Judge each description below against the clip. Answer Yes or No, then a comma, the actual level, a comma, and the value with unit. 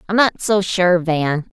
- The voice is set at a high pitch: No, medium, 180 Hz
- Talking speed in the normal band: Yes, average, 195 wpm